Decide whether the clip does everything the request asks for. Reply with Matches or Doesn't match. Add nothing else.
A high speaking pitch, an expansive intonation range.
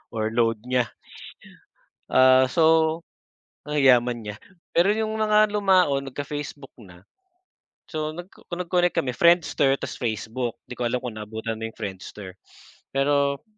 Doesn't match